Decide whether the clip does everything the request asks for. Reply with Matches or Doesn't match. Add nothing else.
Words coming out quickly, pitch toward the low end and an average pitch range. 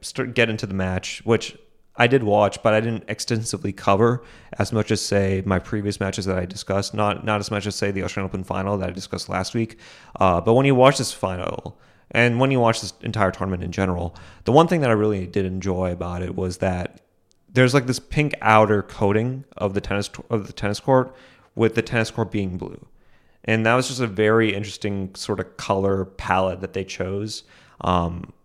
Matches